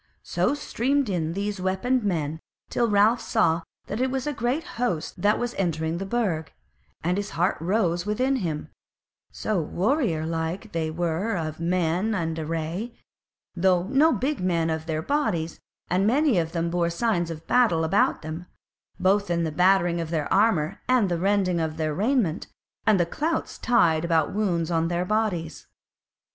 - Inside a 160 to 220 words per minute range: Yes, average, 170 wpm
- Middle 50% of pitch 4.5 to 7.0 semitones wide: Yes, average, 5.1 semitones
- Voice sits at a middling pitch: Yes, medium, 180 Hz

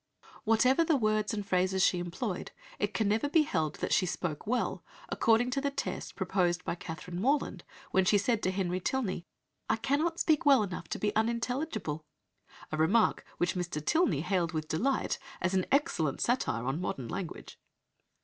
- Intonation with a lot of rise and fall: Yes, wide, 6.0 semitones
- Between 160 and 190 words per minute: Yes, average, 175 wpm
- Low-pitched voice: No, high, 200 Hz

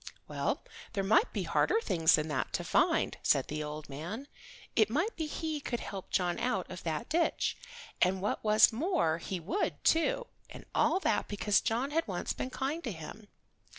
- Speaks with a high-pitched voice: Yes, high, 215 Hz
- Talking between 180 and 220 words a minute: Yes, average, 185 wpm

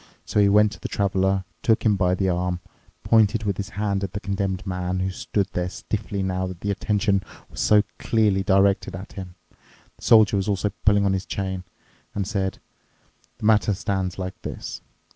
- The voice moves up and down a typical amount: No, narrow, 1.7 semitones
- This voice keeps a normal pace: Yes, average, 180 wpm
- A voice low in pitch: Yes, low, 100 Hz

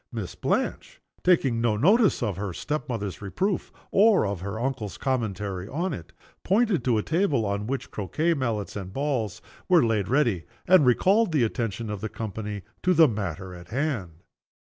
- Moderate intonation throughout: No, wide, 7.1 semitones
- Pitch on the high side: No, low, 115 Hz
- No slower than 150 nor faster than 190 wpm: Yes, average, 170 wpm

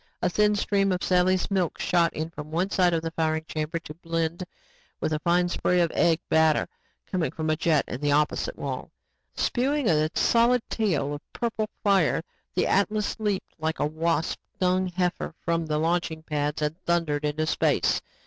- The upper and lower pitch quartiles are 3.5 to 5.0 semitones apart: No, average, 3.1 semitones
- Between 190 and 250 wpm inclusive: No, average, 180 wpm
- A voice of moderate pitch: Yes, medium, 170 Hz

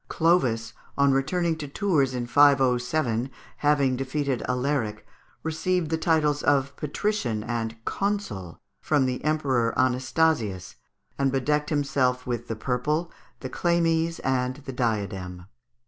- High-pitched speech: No, low, 135 Hz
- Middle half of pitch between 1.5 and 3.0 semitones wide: No, average, 4.1 semitones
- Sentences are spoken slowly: Yes, slow, 125 wpm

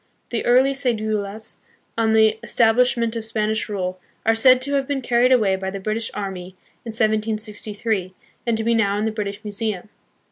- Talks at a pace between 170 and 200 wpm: Yes, average, 175 wpm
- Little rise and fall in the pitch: Yes, narrow, 2.1 semitones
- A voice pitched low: No, high, 220 Hz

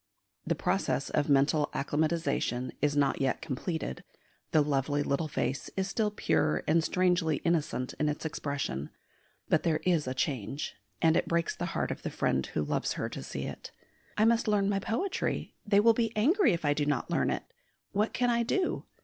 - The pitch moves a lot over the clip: Yes, wide, 6.0 semitones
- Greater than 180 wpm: Yes, average, 190 wpm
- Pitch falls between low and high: Yes, medium, 160 Hz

